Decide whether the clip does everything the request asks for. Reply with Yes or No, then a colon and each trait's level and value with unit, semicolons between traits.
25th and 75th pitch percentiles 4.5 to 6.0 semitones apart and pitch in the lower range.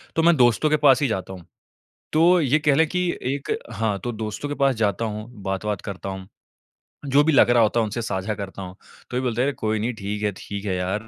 Yes: average, 5.3 semitones; low, 110 Hz